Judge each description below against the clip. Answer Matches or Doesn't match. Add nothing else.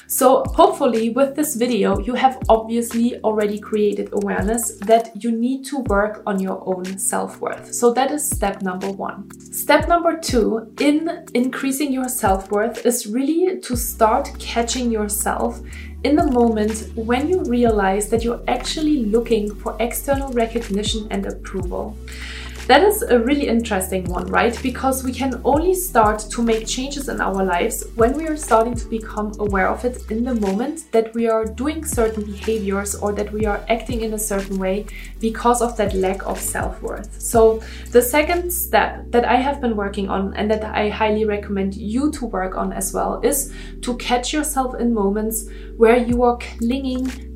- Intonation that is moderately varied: Matches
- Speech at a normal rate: Matches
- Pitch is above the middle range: Matches